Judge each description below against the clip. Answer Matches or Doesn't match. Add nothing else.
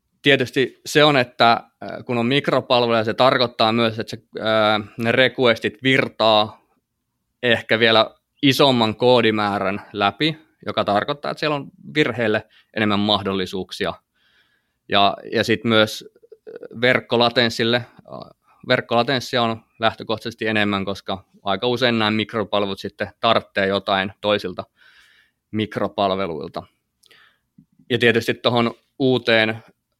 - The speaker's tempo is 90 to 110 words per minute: Matches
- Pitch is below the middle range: Matches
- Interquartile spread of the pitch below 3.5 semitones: Matches